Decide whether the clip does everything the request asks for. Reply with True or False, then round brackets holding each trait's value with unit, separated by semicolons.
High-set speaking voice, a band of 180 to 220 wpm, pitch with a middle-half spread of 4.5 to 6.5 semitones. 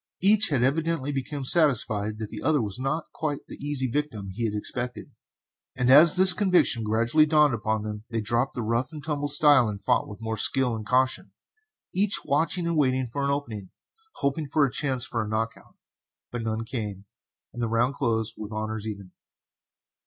False (125 Hz; 190 wpm; 4.9 semitones)